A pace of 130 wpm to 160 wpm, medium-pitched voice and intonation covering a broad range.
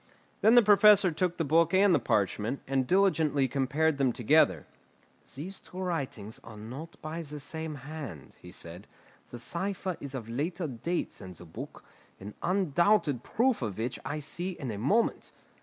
No: average, 170 wpm; medium, 150 Hz; wide, 6.8 semitones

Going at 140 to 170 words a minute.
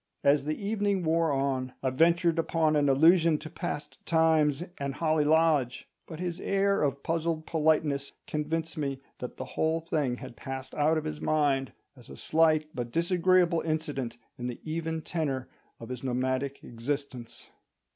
Yes: average, 160 wpm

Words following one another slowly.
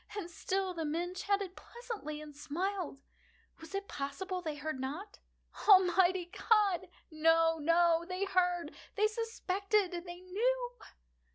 Yes: slow, 110 wpm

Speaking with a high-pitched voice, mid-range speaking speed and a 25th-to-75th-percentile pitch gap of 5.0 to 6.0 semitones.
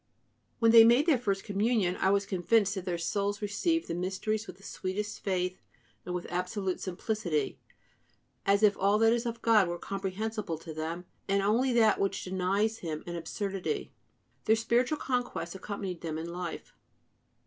No: high, 195 Hz; average, 170 wpm; average, 3.5 semitones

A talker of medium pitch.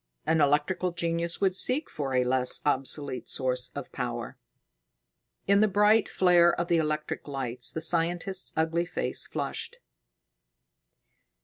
Yes: medium, 165 Hz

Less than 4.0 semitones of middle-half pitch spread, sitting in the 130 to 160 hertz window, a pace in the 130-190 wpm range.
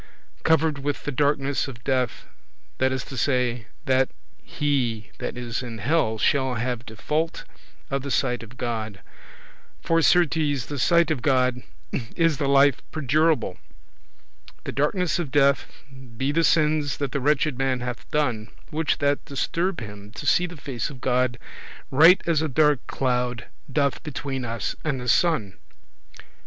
Yes: average, 3.5 semitones; low, 135 Hz; average, 160 wpm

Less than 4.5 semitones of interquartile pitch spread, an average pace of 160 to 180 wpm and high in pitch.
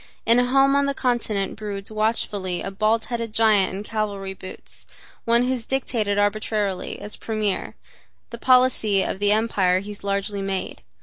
Yes: average, 2.7 semitones; average, 170 wpm; high, 215 Hz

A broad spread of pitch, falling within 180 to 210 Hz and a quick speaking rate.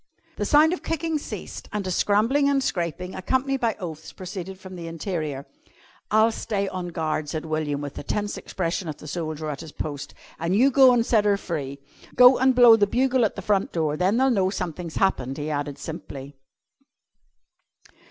No: wide, 6.6 semitones; medium, 185 Hz; average, 190 wpm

